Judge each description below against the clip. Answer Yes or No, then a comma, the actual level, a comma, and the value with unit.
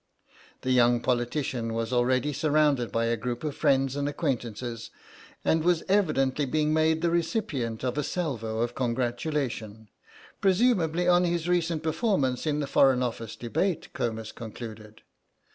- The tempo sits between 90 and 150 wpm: Yes, average, 140 wpm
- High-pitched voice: No, low, 135 Hz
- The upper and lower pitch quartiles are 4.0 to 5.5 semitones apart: Yes, average, 5.1 semitones